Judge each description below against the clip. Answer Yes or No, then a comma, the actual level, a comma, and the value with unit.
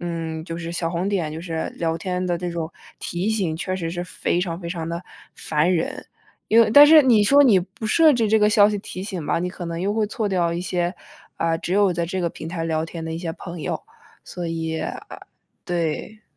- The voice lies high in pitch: No, medium, 175 Hz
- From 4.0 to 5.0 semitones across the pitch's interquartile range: No, average, 3.3 semitones